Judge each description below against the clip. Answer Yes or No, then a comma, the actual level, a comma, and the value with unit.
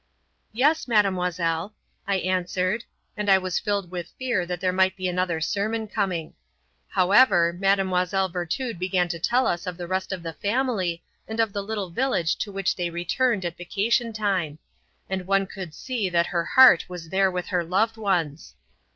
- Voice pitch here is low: No, high, 190 Hz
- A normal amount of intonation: Yes, average, 3.0 semitones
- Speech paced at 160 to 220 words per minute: Yes, average, 175 wpm